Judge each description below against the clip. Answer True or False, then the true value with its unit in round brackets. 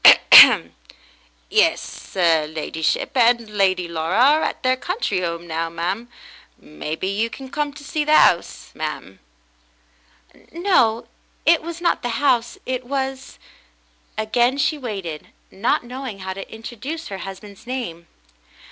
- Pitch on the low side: False (220 Hz)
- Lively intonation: True (7.5 semitones)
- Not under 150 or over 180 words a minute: False (140 wpm)